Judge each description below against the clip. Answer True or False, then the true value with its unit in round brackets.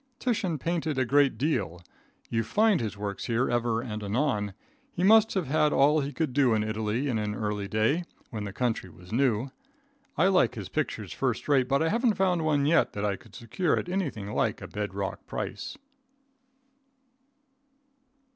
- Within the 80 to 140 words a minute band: False (180 wpm)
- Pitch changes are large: True (6.9 semitones)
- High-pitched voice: False (130 Hz)